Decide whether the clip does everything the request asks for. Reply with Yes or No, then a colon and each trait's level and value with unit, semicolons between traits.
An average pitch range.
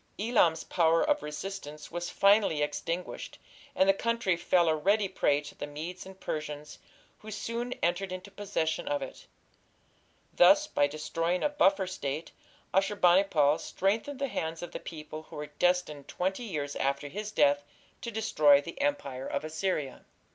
Yes: average, 4.8 semitones